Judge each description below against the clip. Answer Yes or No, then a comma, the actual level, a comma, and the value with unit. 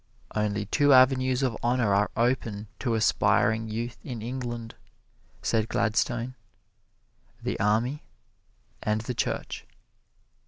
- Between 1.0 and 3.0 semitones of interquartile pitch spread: Yes, average, 2.7 semitones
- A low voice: Yes, low, 115 Hz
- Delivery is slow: Yes, slow, 110 wpm